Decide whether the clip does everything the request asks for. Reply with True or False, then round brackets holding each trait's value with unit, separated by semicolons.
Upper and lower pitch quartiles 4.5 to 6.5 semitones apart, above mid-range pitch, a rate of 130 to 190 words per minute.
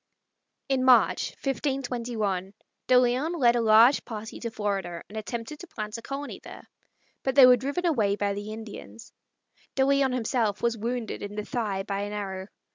False (3.9 semitones; 230 Hz; 175 wpm)